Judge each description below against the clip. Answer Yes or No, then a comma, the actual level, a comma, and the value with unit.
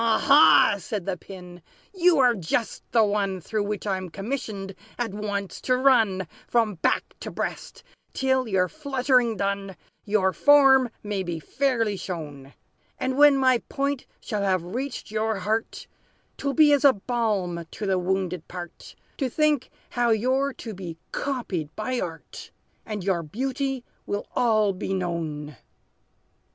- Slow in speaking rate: No, average, 150 wpm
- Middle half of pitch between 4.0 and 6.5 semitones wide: Yes, wide, 5.4 semitones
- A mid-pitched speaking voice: No, high, 215 Hz